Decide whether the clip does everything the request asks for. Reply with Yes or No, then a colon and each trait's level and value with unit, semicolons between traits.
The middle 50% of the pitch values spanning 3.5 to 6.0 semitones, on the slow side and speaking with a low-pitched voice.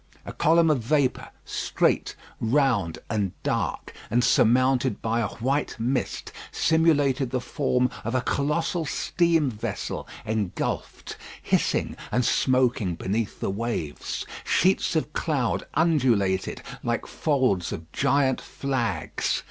Yes: average, 4.6 semitones; slow, 115 wpm; low, 130 Hz